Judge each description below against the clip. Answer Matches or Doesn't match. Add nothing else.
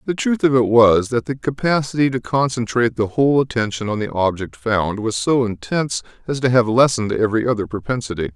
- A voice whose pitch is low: Matches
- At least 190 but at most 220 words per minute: Matches